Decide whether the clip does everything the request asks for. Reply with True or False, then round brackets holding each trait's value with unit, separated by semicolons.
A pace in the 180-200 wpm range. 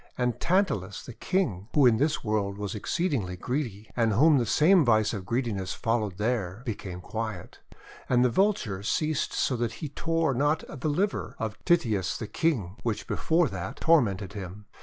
False (170 wpm)